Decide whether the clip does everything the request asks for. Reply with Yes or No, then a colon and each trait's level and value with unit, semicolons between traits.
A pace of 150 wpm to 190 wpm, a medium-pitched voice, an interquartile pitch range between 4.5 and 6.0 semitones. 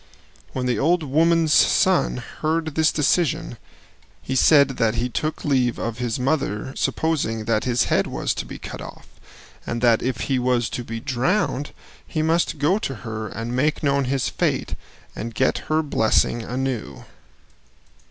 No: average, 160 wpm; low, 130 Hz; average, 4.8 semitones